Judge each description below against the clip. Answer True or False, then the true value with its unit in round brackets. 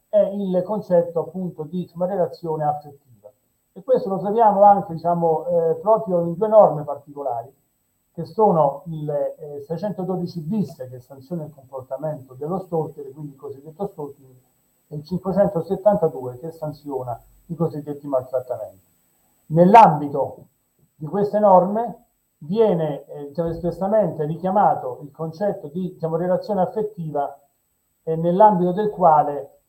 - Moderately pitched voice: True (165 Hz)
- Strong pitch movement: False (4.5 semitones)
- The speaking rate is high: False (130 wpm)